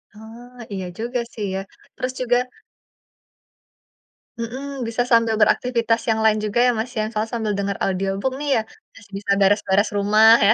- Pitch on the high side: Yes, high, 225 Hz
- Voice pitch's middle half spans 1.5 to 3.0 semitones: Yes, narrow, 2.6 semitones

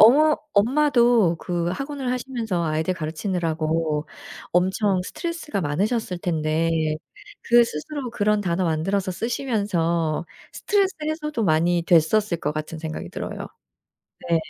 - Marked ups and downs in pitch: Yes, wide, 6.5 semitones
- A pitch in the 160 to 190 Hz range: Yes, medium, 185 Hz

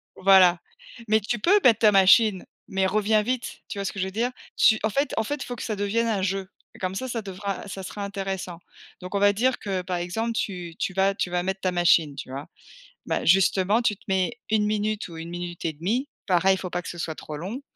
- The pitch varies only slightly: No, average, 3.0 semitones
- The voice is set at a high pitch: Yes, high, 195 Hz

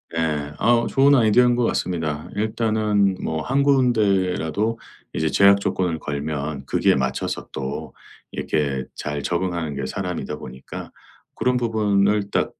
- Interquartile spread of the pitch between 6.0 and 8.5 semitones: Yes, wide, 6.4 semitones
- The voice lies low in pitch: Yes, very low, 95 Hz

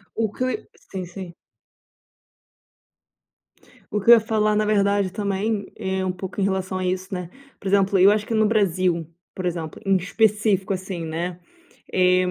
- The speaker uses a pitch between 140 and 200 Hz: Yes, high, 190 Hz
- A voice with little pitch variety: Yes, narrow, 2.3 semitones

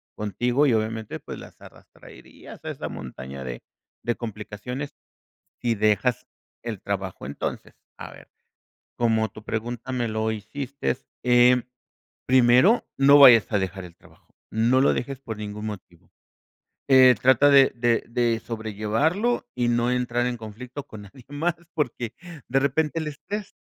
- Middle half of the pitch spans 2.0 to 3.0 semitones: No, average, 3.4 semitones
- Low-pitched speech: Yes, low, 120 Hz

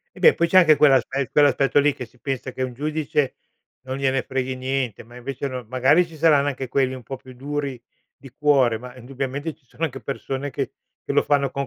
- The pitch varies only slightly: Yes, narrow, 2.1 semitones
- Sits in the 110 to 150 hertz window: Yes, low, 135 Hz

